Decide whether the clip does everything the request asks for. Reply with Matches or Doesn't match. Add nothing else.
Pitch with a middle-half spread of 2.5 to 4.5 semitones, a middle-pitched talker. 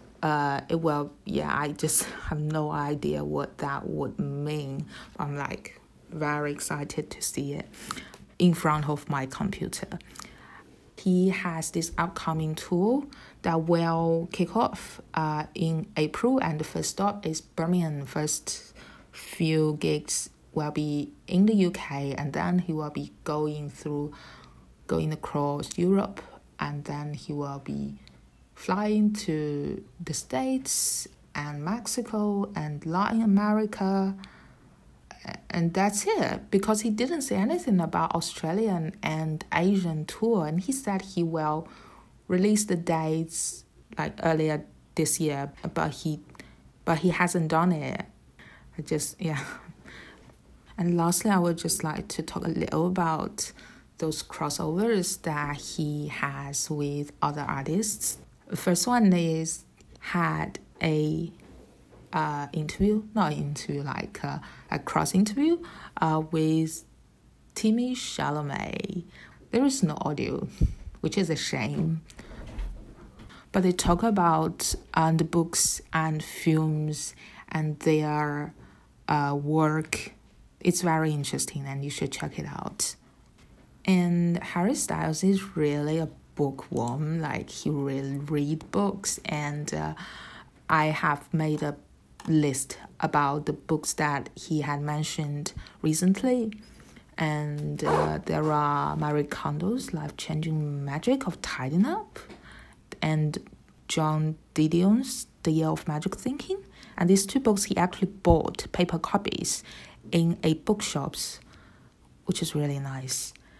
Matches